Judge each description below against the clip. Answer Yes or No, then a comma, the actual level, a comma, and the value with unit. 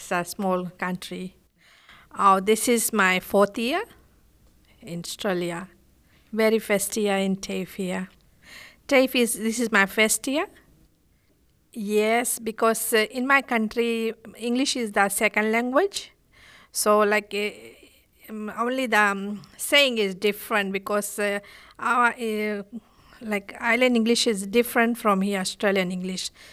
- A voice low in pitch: No, high, 215 Hz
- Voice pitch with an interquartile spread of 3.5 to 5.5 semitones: No, average, 3.0 semitones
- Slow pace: Yes, slow, 130 wpm